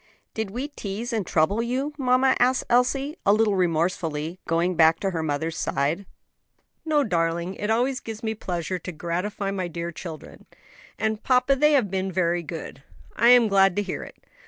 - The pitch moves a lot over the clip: Yes, wide, 6.0 semitones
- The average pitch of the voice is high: Yes, high, 195 Hz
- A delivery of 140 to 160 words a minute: No, average, 180 wpm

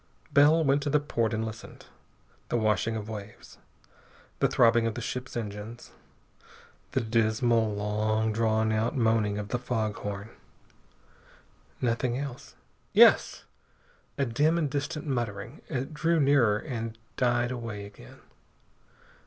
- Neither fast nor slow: No, slow, 130 wpm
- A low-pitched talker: Yes, low, 115 Hz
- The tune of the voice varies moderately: Yes, average, 3.3 semitones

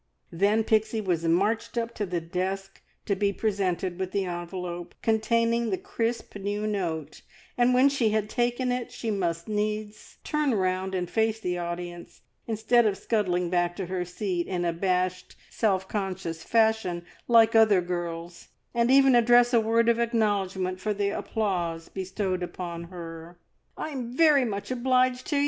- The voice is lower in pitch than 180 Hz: No, high, 200 Hz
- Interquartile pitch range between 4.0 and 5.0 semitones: Yes, average, 4.3 semitones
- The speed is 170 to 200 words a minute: No, average, 160 wpm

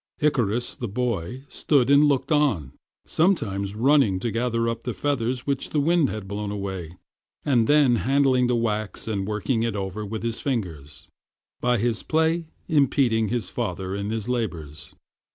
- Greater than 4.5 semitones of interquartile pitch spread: Yes, average, 4.9 semitones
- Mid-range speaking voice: No, low, 115 Hz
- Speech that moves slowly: No, average, 160 wpm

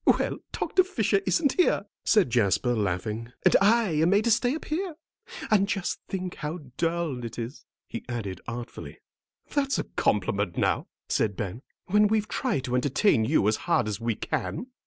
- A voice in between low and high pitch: Yes, medium, 160 Hz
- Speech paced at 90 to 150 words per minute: No, average, 175 wpm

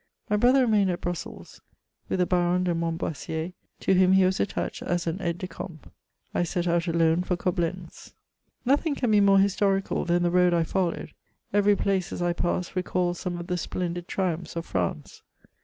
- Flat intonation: Yes, narrow, 1.9 semitones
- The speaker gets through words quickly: No, average, 190 wpm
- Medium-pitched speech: Yes, medium, 180 Hz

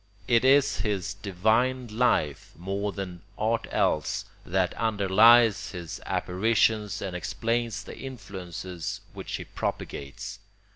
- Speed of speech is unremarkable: No, slow, 110 wpm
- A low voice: Yes, low, 100 Hz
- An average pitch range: Yes, average, 4.0 semitones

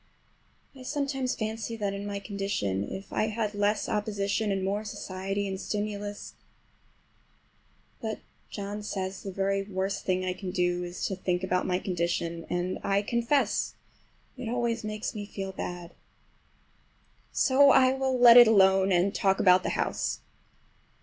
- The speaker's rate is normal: Yes, average, 150 wpm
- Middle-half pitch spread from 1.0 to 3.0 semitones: Yes, narrow, 2.6 semitones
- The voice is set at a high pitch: Yes, high, 200 Hz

